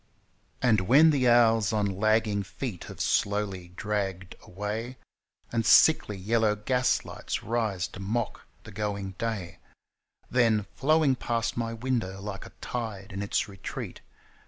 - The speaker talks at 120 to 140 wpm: Yes, slow, 135 wpm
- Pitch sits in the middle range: No, low, 110 Hz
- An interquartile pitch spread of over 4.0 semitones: No, average, 3.0 semitones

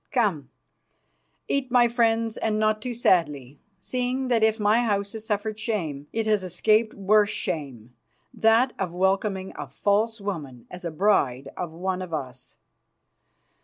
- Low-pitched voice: No, high, 205 Hz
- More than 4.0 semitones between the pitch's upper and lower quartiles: Yes, average, 4.8 semitones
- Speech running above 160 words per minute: No, average, 150 wpm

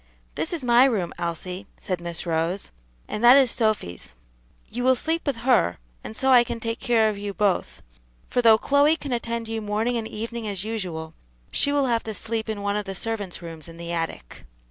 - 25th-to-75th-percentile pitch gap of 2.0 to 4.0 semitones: No, average, 4.5 semitones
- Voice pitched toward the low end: No, high, 220 Hz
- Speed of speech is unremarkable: No, fast, 210 wpm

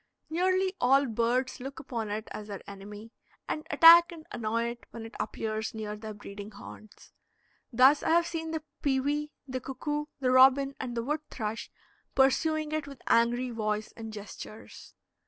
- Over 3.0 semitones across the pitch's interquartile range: Yes, average, 5.3 semitones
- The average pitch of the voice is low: No, very high, 255 Hz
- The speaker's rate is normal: Yes, average, 165 wpm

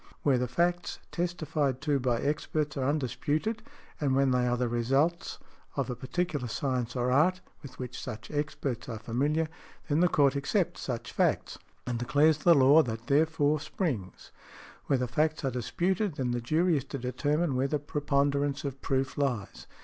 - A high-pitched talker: No, medium, 140 Hz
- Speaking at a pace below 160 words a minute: No, average, 170 wpm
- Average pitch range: Yes, average, 3.6 semitones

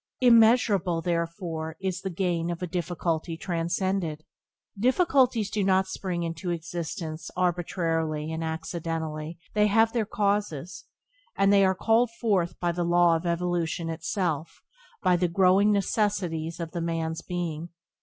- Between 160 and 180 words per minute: No, slow, 135 wpm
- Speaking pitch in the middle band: Yes, medium, 175 Hz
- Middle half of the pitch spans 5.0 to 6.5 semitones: No, average, 3.0 semitones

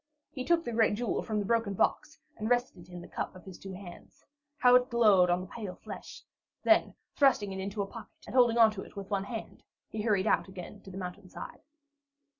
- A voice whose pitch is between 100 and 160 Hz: No, high, 205 Hz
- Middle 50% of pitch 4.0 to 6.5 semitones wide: No, average, 3.5 semitones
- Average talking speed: No, fast, 225 wpm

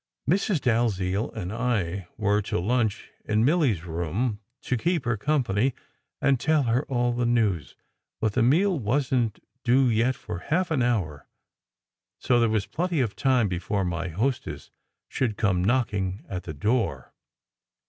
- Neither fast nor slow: Yes, average, 160 wpm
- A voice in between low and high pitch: No, low, 115 Hz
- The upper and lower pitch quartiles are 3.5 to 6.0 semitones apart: Yes, average, 4.8 semitones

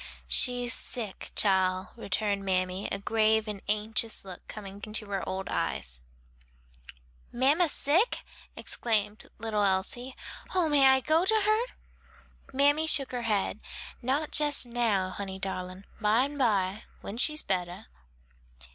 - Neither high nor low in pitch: No, high, 220 Hz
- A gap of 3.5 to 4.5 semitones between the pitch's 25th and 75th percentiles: No, wide, 5.4 semitones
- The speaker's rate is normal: No, slow, 130 wpm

